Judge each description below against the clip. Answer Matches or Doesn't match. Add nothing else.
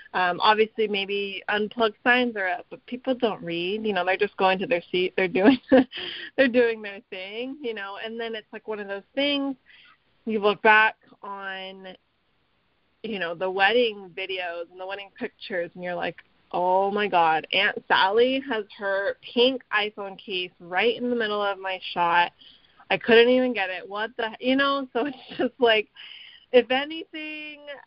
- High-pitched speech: Matches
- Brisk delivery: Doesn't match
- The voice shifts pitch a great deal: Doesn't match